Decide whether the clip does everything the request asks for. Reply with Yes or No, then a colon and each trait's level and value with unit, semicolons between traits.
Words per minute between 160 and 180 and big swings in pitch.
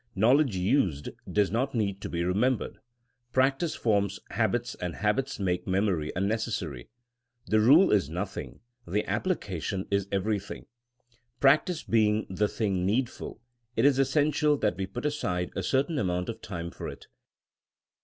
No: average, 145 wpm; wide, 5.9 semitones